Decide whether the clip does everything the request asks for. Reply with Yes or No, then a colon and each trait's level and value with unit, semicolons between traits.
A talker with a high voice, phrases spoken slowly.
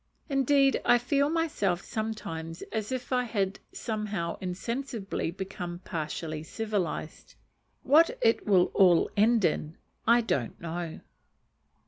Yes: high, 205 Hz; slow, 115 wpm